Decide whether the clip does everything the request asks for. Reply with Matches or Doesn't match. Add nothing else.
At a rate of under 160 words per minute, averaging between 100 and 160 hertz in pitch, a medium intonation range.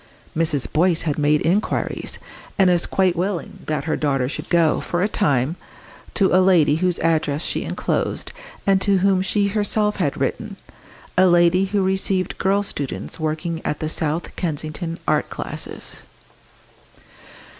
Doesn't match